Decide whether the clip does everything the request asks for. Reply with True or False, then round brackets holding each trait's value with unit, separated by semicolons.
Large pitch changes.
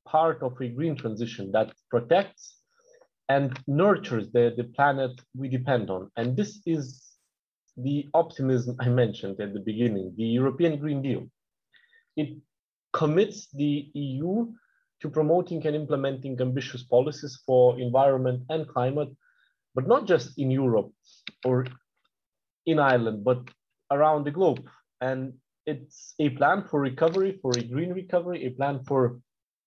False (3.9 semitones)